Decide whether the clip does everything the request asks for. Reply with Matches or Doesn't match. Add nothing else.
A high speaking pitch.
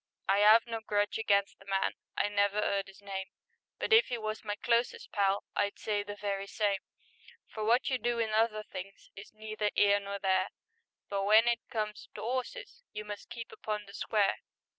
Matches